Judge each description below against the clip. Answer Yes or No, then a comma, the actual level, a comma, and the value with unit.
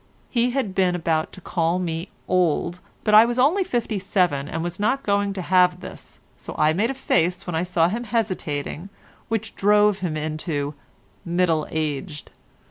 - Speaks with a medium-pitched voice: Yes, medium, 180 Hz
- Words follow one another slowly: No, average, 175 wpm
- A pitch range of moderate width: Yes, average, 4.3 semitones